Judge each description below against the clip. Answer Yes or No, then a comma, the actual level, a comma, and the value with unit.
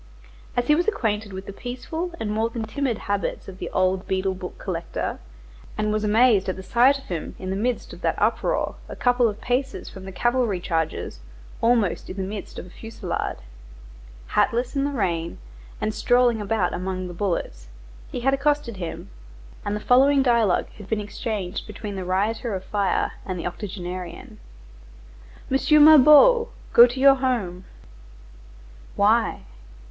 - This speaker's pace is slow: No, average, 165 wpm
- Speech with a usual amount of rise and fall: Yes, average, 4.8 semitones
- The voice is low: No, high, 215 Hz